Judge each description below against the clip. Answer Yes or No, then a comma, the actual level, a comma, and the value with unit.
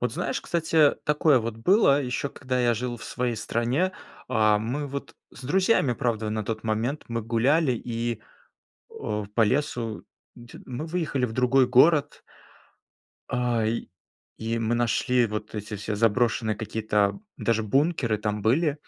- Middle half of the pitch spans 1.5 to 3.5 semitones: No, average, 4.0 semitones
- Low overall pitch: Yes, low, 120 Hz